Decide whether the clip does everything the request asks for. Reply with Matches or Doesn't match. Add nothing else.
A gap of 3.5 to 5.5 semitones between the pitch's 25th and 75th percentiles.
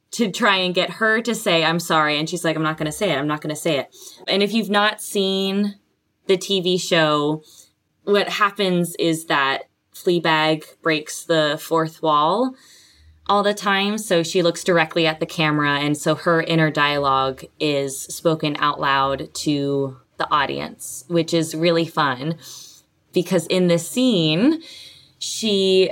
Matches